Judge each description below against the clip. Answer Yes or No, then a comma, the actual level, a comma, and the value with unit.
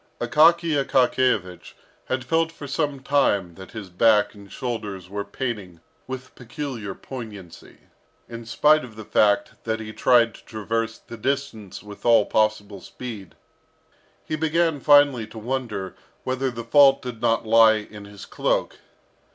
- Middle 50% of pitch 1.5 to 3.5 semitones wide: No, average, 4.2 semitones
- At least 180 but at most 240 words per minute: No, average, 145 wpm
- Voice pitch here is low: Yes, low, 115 Hz